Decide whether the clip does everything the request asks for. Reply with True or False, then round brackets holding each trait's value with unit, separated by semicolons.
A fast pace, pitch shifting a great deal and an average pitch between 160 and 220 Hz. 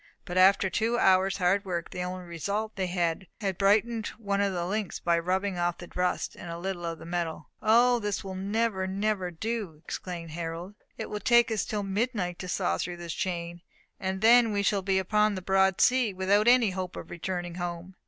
False (210 wpm; 3.0 semitones; 190 Hz)